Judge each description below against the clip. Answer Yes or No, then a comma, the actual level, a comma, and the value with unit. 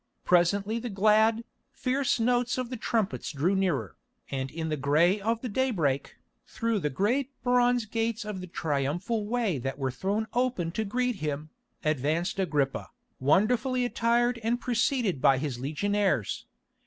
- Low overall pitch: No, high, 205 Hz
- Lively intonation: Yes, wide, 7.5 semitones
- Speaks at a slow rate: No, average, 150 wpm